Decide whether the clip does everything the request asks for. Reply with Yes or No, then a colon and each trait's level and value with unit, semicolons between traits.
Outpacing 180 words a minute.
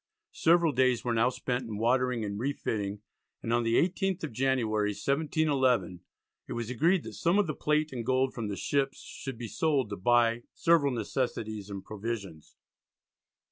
No: average, 175 wpm